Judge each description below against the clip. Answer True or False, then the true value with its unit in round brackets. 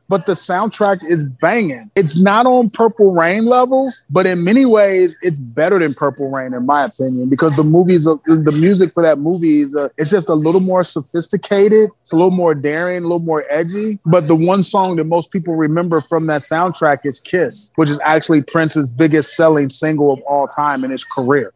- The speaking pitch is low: False (165 Hz)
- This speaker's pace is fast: True (210 wpm)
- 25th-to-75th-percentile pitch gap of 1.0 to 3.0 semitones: False (3.9 semitones)